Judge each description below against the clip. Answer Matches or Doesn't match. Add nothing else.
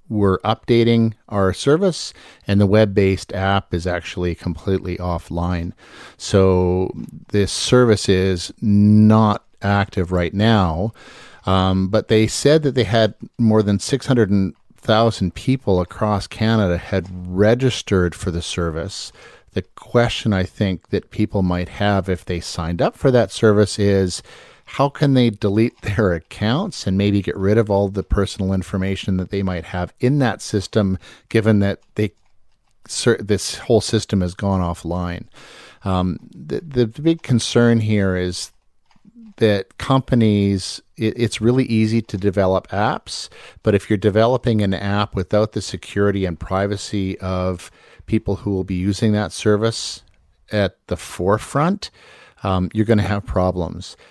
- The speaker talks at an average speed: Matches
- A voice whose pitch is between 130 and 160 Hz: Doesn't match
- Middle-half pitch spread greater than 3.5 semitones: Doesn't match